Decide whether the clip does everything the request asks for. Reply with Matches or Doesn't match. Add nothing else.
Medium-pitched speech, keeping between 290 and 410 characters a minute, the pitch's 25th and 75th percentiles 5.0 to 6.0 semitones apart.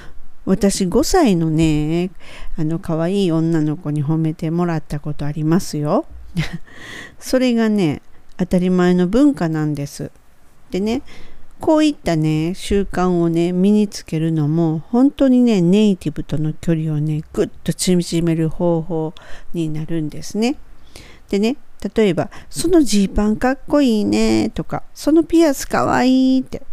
Doesn't match